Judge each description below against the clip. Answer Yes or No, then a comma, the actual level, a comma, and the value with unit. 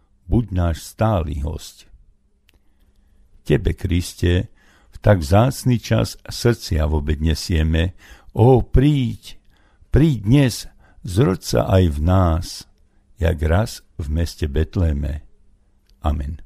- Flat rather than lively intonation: No, average, 5.1 semitones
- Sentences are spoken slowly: Yes, slow, 105 wpm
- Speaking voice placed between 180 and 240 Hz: No, very low, 90 Hz